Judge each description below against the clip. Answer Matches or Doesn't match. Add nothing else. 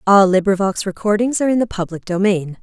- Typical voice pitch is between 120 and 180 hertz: Doesn't match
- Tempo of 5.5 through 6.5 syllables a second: Matches